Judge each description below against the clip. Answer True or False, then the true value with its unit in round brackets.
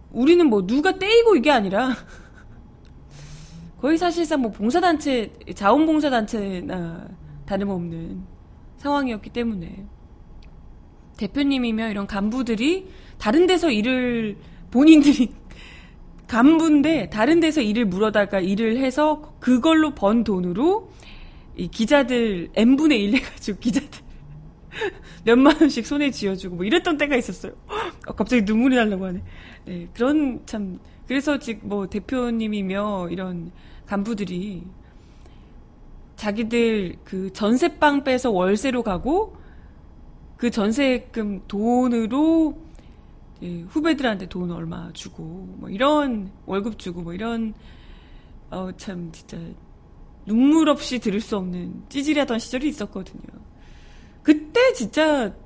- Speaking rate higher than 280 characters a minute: False (245 characters per minute)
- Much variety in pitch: True (6.6 semitones)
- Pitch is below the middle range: False (230 Hz)